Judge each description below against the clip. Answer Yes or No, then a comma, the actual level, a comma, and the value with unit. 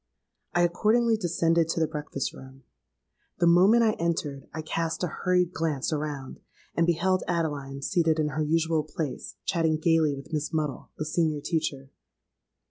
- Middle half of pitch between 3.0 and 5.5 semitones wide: No, narrow, 2.4 semitones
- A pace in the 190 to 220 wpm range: No, average, 155 wpm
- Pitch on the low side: No, medium, 160 Hz